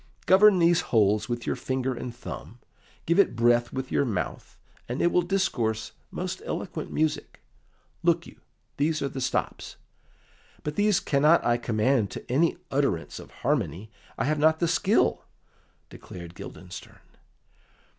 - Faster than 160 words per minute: No, average, 145 wpm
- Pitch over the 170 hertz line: No, low, 130 Hz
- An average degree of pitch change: No, wide, 5.7 semitones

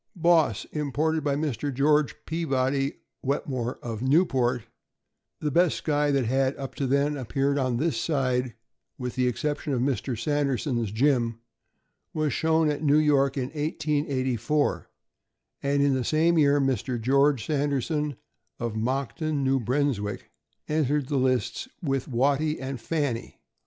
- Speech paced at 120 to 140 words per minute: Yes, slow, 135 wpm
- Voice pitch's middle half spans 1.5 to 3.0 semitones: Yes, average, 2.7 semitones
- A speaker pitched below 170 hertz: Yes, medium, 140 Hz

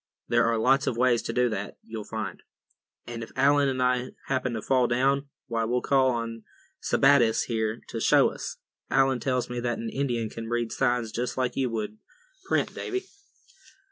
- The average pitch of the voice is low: Yes, low, 120 Hz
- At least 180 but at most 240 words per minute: Yes, average, 185 wpm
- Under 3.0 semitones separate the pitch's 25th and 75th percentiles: Yes, narrow, 2.4 semitones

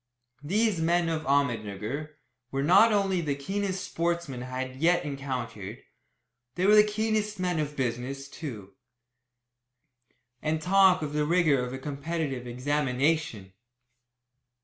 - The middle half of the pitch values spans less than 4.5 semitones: No, average, 5.2 semitones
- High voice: No, medium, 150 Hz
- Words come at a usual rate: No, slow, 125 wpm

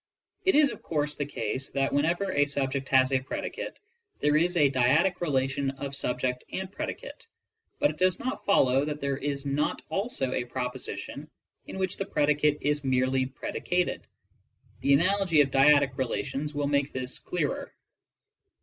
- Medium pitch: Yes, medium, 145 Hz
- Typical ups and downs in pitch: Yes, average, 3.8 semitones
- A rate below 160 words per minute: No, average, 165 wpm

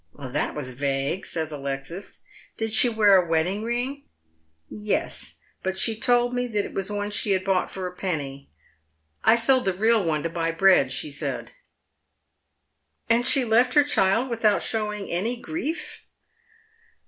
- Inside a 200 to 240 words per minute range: No, average, 175 wpm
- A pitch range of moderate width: No, wide, 7.2 semitones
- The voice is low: No, high, 195 Hz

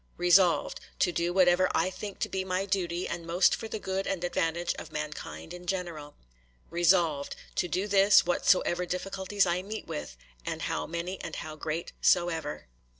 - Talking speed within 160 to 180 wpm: Yes, average, 170 wpm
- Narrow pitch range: Yes, narrow, 2.1 semitones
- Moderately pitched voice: Yes, medium, 175 Hz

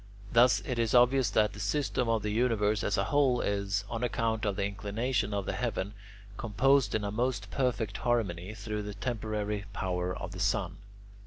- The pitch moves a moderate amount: Yes, average, 3.2 semitones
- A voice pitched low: Yes, low, 110 Hz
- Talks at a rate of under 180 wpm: No, average, 185 wpm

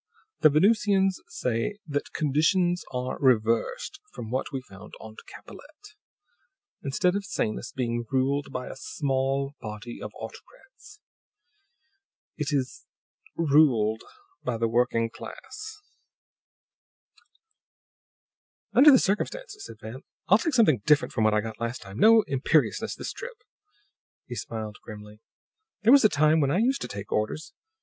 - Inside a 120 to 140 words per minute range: Yes, slow, 135 wpm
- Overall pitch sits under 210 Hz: Yes, medium, 140 Hz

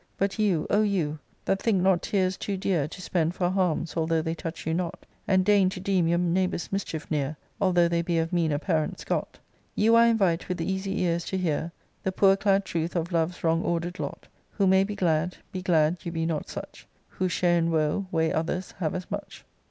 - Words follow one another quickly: Yes, fast, 215 wpm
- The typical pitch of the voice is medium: Yes, medium, 175 Hz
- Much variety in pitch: No, narrow, 2.6 semitones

